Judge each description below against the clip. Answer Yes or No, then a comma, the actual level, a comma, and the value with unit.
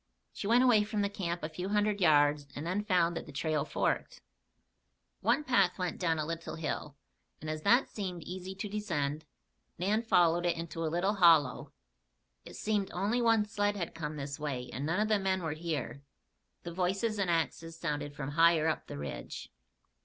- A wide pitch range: No, average, 4.6 semitones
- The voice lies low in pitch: No, medium, 170 Hz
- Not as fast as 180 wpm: No, average, 190 wpm